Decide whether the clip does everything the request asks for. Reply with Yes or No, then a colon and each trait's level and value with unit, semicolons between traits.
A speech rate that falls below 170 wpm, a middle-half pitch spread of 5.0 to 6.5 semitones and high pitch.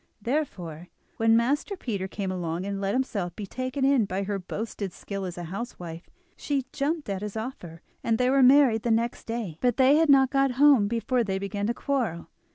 No: average, 200 wpm; average, 5.3 semitones; high, 225 Hz